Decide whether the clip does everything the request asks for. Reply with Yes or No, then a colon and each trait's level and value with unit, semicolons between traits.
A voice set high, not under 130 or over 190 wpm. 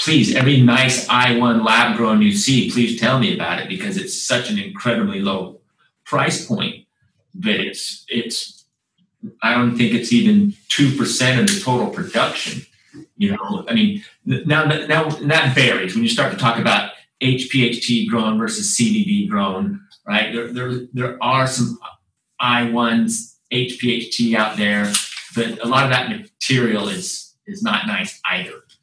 No: low, 130 Hz; average, 180 wpm